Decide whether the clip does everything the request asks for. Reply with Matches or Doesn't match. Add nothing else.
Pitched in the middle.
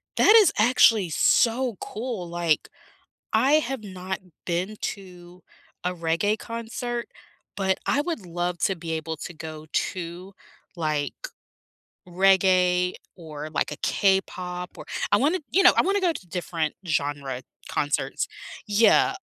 Matches